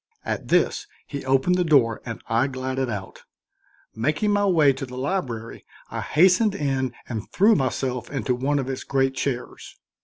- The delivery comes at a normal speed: Yes, average, 165 wpm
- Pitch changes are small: No, average, 3.4 semitones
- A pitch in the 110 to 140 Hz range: Yes, low, 135 Hz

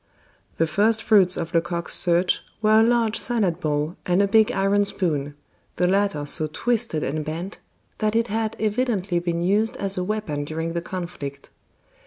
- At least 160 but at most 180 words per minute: Yes, average, 170 wpm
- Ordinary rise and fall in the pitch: Yes, average, 4.5 semitones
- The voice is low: No, medium, 185 Hz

